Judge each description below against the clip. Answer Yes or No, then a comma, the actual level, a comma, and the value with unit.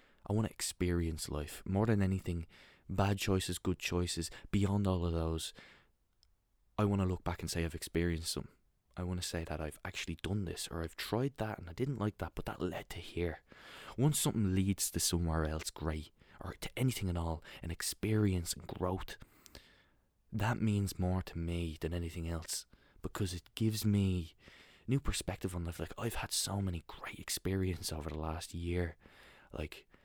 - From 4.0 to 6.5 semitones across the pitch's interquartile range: No, average, 3.3 semitones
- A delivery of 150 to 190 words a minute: Yes, average, 185 wpm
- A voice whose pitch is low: Yes, very low, 90 Hz